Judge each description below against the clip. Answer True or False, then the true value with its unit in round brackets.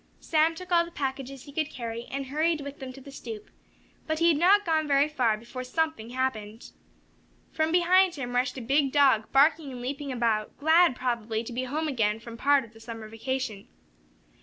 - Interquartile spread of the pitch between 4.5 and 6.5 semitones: True (4.8 semitones)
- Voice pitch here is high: True (270 Hz)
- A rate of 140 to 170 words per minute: False (200 wpm)